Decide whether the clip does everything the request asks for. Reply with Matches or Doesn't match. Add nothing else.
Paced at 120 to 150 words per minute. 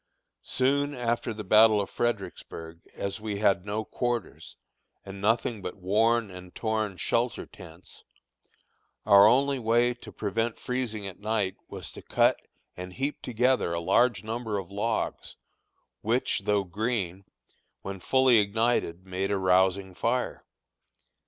Matches